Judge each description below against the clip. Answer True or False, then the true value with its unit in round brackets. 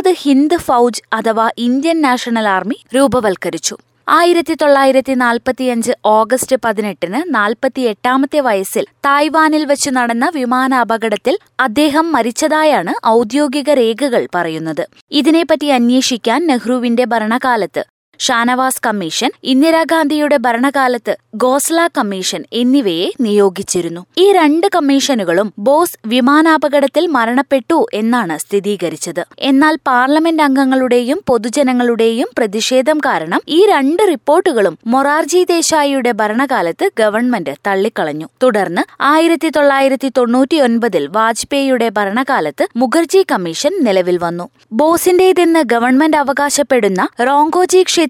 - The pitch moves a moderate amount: True (4.8 semitones)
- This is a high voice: True (260 Hz)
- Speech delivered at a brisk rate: False (90 wpm)